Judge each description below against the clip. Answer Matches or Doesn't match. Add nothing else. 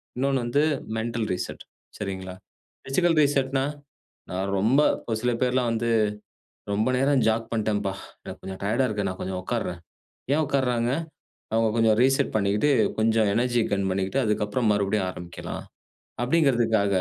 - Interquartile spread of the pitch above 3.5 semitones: Matches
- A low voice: Matches